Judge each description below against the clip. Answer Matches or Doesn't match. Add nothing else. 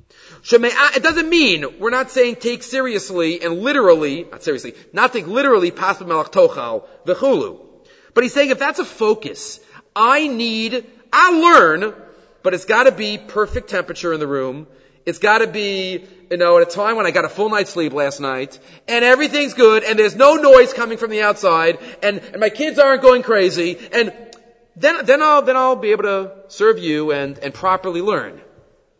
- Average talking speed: Matches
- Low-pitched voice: Doesn't match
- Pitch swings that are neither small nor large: Doesn't match